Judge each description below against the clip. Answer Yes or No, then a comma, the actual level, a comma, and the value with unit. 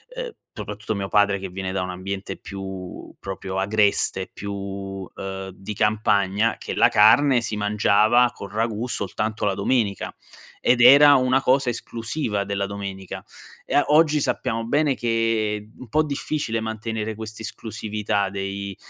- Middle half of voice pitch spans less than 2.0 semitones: No, average, 2.7 semitones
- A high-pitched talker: No, low, 105 Hz